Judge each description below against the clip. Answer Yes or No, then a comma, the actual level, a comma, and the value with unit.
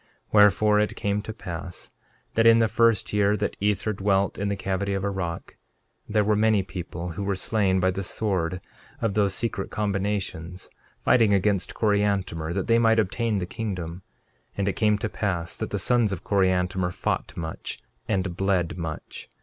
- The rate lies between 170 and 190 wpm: Yes, average, 180 wpm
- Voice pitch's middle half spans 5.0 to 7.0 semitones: No, narrow, 2.4 semitones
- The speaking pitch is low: Yes, low, 100 Hz